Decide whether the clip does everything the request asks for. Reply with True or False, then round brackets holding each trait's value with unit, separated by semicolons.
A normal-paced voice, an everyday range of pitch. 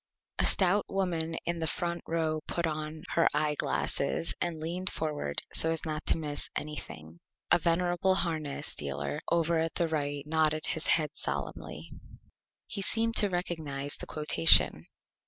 False (155 wpm; 2.3 semitones)